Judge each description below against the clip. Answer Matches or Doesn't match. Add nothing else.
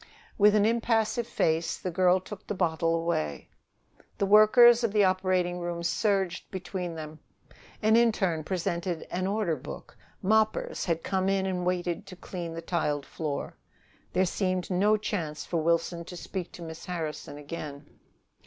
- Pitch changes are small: Doesn't match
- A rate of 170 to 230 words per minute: Doesn't match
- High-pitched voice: Doesn't match